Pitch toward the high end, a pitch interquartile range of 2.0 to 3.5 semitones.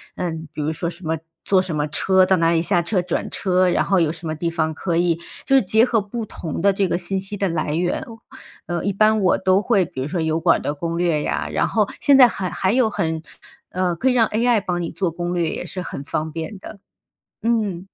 No: medium, 180 Hz; average, 3.2 semitones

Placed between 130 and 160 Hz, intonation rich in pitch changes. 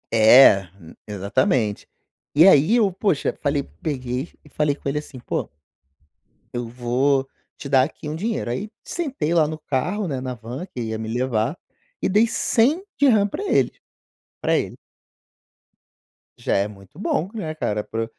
Yes: medium, 140 Hz; wide, 7.1 semitones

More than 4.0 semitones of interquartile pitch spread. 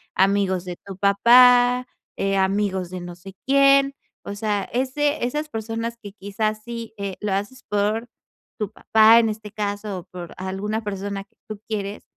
No: average, 2.9 semitones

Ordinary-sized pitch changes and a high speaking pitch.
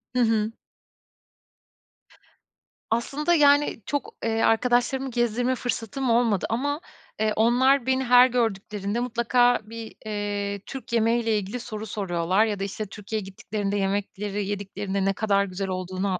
Yes: average, 3.4 semitones; high, 220 Hz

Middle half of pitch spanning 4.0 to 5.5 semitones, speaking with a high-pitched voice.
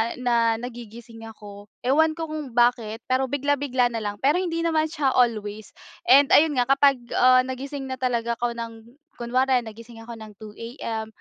No: average, 3.2 semitones; high, 245 Hz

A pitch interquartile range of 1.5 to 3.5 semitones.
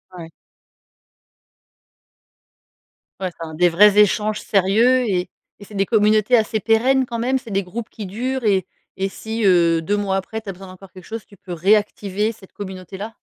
Yes: average, 2.8 semitones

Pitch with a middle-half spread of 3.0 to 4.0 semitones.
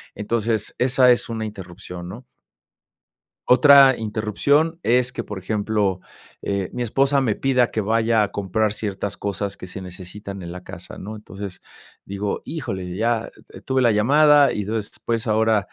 Yes: average, 3.6 semitones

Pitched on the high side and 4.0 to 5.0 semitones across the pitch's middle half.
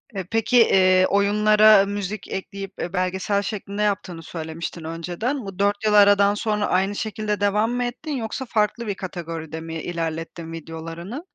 No: high, 200 Hz; average, 3.4 semitones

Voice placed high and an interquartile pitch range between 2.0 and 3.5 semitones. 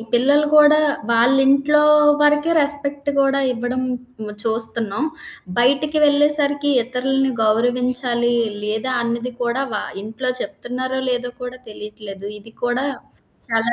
Yes: very high, 255 Hz; average, 3.1 semitones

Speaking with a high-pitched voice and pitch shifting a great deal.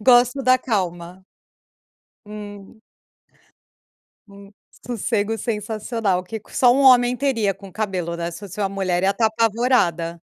No: high, 210 Hz; average, 3.9 semitones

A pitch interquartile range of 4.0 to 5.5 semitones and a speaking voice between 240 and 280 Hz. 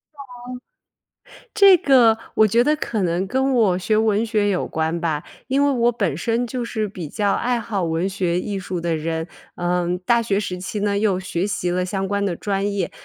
No: average, 4.3 semitones; high, 200 Hz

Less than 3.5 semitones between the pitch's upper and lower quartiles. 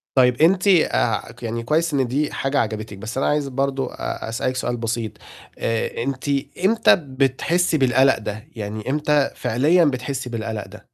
No: average, 4.2 semitones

